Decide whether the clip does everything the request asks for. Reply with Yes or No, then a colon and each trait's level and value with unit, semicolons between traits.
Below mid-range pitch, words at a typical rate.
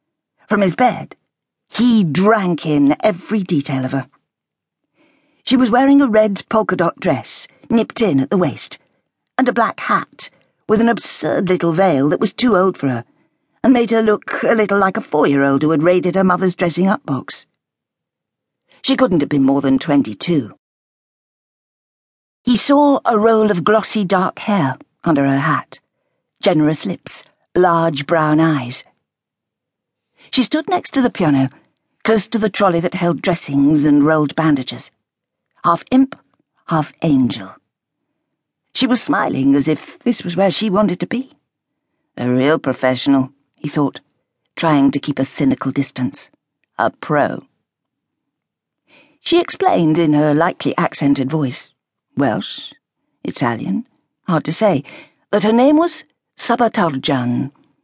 No: medium, 170 Hz; average, 150 wpm